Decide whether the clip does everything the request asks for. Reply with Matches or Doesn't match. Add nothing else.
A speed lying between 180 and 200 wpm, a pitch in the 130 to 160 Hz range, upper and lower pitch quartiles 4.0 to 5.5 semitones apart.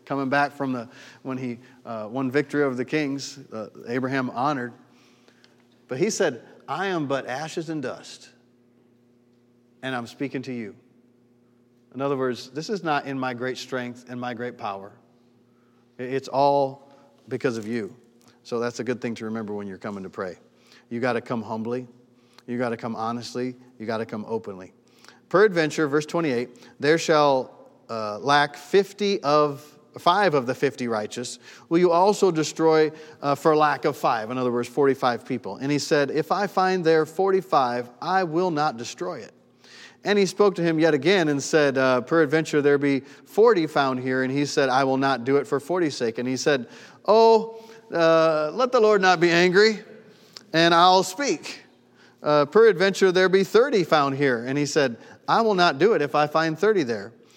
Matches